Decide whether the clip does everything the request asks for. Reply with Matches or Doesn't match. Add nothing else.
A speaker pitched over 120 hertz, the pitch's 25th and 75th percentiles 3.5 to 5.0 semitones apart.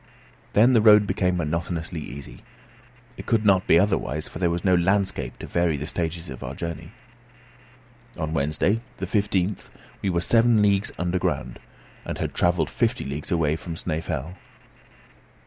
Doesn't match